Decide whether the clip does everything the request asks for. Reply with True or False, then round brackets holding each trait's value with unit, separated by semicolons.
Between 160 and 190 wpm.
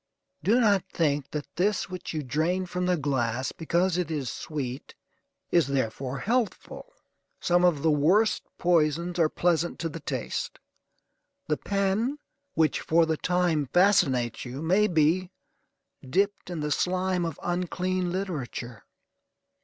False (140 wpm)